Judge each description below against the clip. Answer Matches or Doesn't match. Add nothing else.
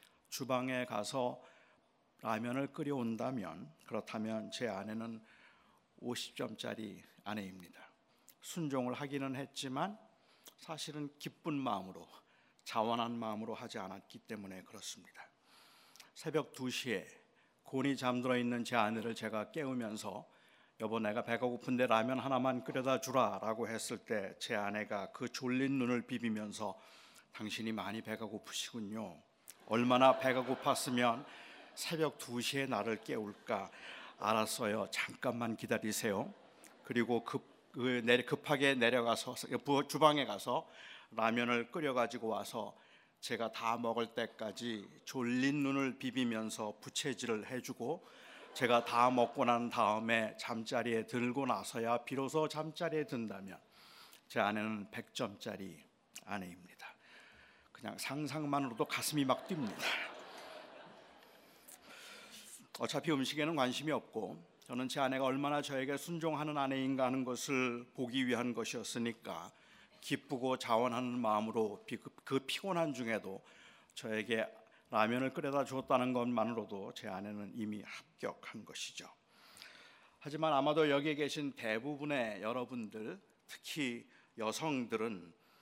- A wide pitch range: Doesn't match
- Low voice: Matches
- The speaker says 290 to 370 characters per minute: Doesn't match